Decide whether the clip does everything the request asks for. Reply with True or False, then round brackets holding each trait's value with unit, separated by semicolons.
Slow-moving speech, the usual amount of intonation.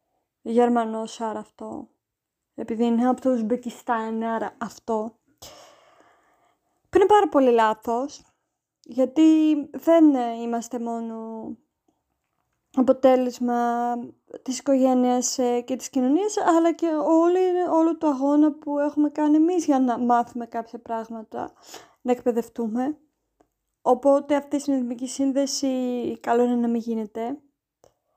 True (110 wpm; 3.7 semitones)